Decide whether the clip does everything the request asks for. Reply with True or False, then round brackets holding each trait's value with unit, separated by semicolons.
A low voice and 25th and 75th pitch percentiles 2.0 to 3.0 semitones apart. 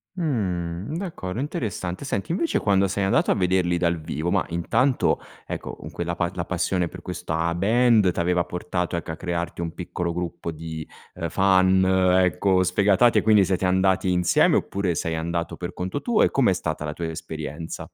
True (90 Hz; 2.4 semitones)